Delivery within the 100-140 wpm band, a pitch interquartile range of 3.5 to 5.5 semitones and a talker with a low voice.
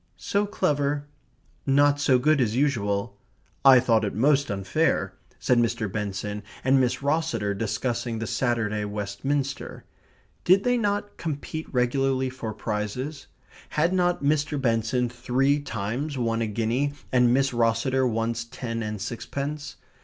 Yes: slow, 135 wpm; average, 4.2 semitones; low, 125 Hz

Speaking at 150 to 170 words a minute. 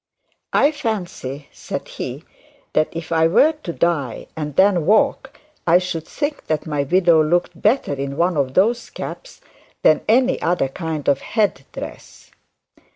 Yes: average, 155 wpm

